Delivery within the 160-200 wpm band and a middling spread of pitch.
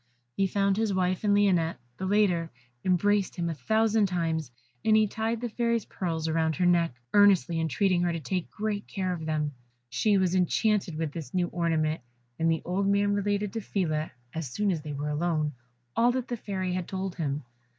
Yes: average, 195 wpm; average, 3.8 semitones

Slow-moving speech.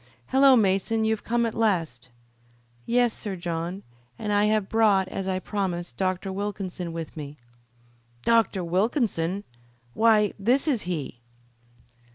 Yes: slow, 130 wpm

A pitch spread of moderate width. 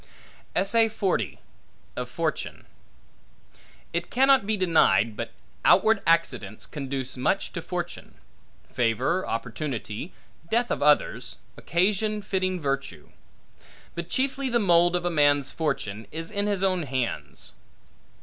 No: wide, 6.8 semitones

